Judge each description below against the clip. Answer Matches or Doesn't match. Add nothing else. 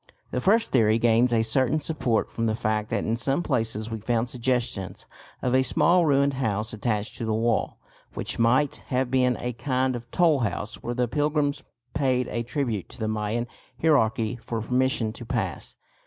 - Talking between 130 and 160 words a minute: Doesn't match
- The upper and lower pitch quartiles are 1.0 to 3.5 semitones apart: Matches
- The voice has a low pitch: Matches